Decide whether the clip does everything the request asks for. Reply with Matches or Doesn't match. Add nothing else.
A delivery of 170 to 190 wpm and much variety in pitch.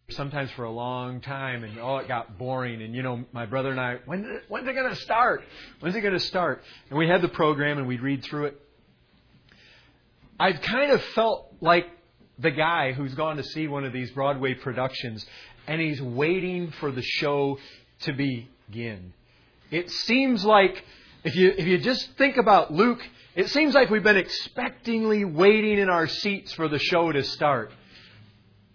Matches